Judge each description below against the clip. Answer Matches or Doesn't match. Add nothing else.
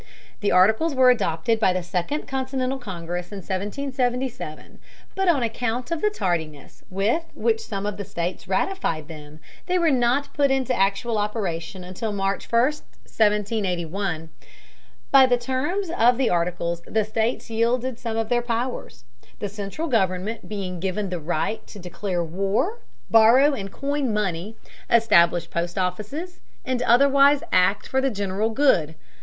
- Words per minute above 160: Doesn't match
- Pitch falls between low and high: Doesn't match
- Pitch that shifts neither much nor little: Doesn't match